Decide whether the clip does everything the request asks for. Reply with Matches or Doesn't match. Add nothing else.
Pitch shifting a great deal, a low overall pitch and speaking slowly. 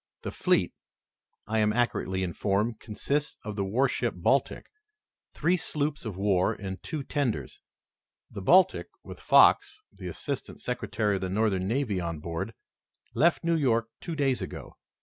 Doesn't match